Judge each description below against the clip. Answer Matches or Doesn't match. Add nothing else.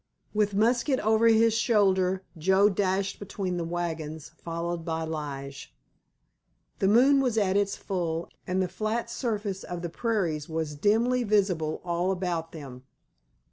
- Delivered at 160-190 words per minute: Doesn't match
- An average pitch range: Matches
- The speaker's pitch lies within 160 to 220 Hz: Matches